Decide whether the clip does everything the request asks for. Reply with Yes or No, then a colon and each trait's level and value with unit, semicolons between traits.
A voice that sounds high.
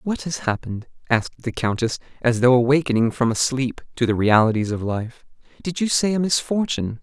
No: low, 130 Hz